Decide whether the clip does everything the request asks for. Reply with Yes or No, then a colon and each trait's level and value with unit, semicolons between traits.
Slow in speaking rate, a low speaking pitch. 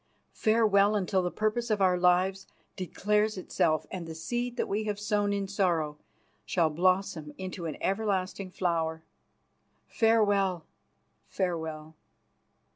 No: slow, 120 wpm; high, 190 Hz